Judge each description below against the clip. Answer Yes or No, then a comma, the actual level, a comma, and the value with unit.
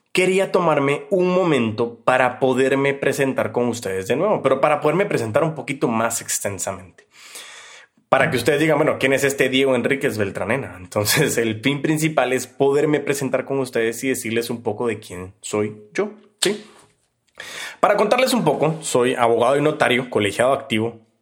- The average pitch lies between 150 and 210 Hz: No, low, 135 Hz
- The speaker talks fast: No, average, 165 wpm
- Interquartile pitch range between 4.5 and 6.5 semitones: No, average, 4.1 semitones